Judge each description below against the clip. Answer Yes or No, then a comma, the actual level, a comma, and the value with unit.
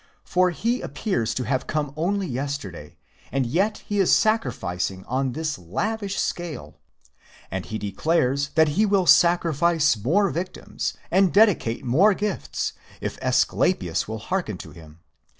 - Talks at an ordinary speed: Yes, average, 150 wpm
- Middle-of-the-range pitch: Yes, medium, 155 Hz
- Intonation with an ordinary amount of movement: No, wide, 8.0 semitones